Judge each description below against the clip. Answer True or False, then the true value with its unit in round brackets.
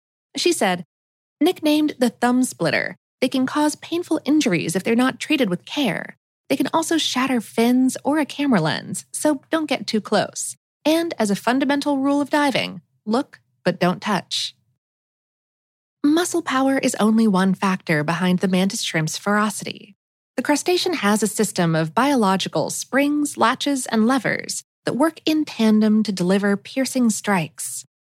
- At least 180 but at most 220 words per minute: False (155 wpm)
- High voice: True (240 Hz)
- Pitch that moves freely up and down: True (6.6 semitones)